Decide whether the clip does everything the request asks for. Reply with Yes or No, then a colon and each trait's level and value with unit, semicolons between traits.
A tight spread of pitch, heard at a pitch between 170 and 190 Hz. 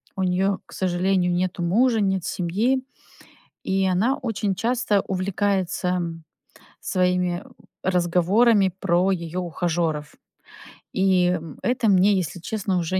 Yes: narrow, 2.0 semitones; medium, 185 Hz